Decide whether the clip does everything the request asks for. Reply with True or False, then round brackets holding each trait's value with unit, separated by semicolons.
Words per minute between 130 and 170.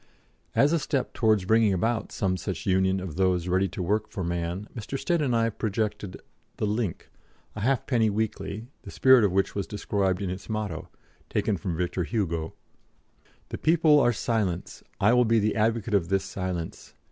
False (180 wpm)